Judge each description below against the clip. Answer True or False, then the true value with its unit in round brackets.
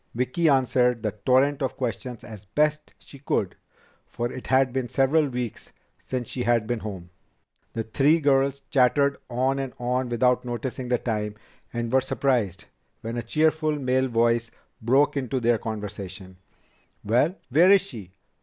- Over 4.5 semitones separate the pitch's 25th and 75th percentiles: False (2.9 semitones)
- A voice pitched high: False (125 Hz)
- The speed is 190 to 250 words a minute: False (155 wpm)